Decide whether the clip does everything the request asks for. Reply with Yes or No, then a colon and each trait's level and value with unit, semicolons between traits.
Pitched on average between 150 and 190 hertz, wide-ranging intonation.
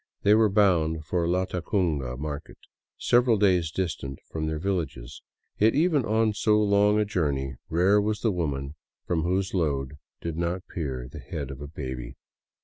No: very low, 85 Hz; wide, 5.9 semitones